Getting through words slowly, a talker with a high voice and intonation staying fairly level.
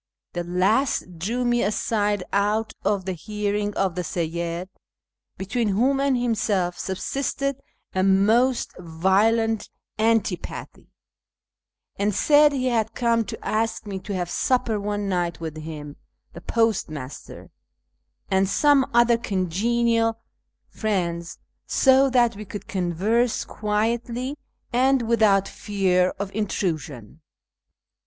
No: slow, 115 wpm; high, 210 Hz; average, 4.3 semitones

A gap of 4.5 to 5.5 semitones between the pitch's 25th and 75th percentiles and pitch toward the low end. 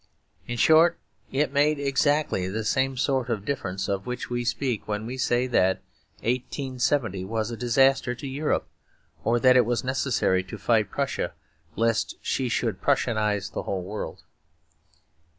No: average, 3.8 semitones; low, 120 Hz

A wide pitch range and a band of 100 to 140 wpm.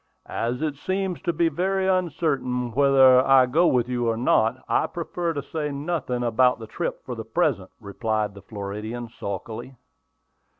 No: wide, 6.0 semitones; average, 165 wpm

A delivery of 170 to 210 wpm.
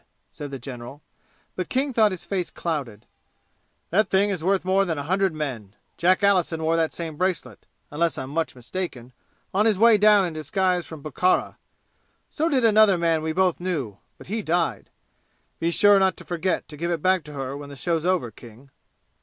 Yes: average, 195 wpm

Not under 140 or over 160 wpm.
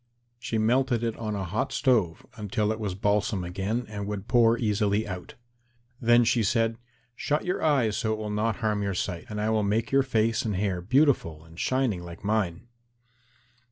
No: average, 190 wpm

